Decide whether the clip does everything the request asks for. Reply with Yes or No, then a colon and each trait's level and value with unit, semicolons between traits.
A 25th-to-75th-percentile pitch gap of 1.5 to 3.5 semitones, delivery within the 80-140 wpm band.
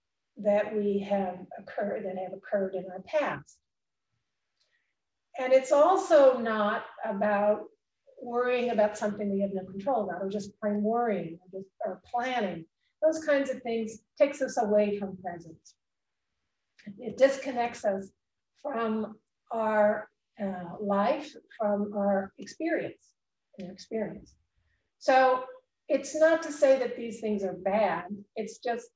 No: average, 4.2 semitones; slow, 135 wpm